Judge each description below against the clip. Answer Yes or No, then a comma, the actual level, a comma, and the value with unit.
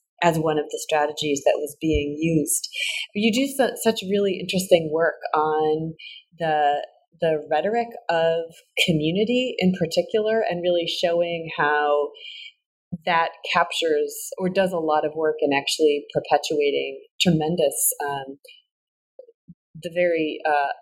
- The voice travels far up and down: Yes, wide, 6.7 semitones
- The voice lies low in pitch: No, medium, 170 Hz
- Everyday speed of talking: No, slow, 125 wpm